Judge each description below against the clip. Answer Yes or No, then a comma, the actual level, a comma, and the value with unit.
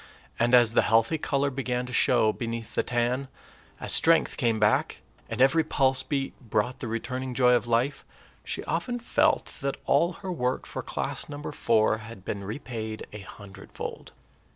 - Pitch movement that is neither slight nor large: Yes, average, 3.3 semitones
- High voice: No, low, 125 Hz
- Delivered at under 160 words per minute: No, average, 170 wpm